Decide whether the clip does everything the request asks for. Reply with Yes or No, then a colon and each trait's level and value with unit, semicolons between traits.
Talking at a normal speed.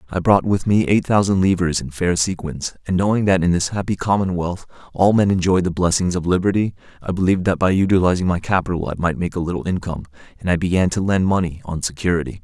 No: fast, 215 wpm